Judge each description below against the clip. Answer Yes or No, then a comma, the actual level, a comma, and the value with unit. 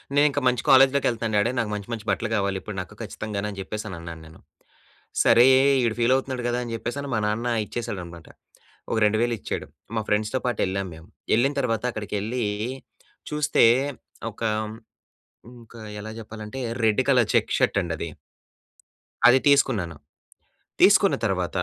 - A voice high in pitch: No, low, 110 Hz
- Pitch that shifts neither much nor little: Yes, average, 3.5 semitones